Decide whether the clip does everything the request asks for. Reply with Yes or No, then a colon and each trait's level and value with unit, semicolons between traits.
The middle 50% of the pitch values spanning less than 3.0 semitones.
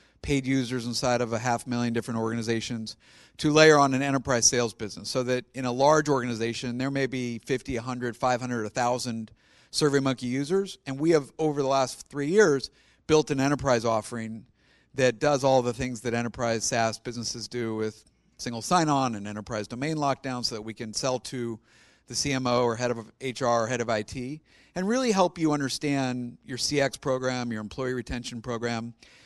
Yes: narrow, 2.6 semitones